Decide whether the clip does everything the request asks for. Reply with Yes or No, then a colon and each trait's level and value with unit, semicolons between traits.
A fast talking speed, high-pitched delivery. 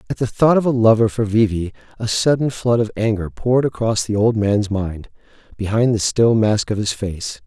No: fast, 215 wpm; low, 110 Hz